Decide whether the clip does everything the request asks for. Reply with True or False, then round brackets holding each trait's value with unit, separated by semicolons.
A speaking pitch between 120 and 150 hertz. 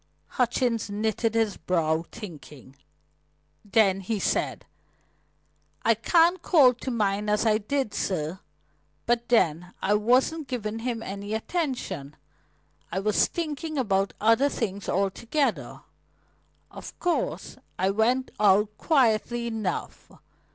False (220 Hz)